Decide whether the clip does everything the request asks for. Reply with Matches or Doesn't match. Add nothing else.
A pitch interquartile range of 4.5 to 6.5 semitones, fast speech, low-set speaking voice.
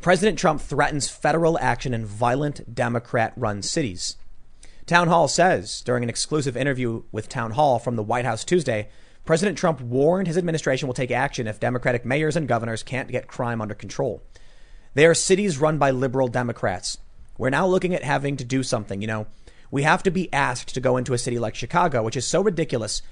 Doesn't match